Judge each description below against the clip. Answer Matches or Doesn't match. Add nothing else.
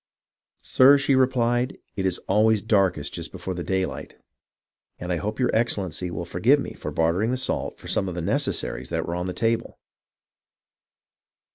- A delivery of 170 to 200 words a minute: Matches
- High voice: Doesn't match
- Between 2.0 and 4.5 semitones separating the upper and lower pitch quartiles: Doesn't match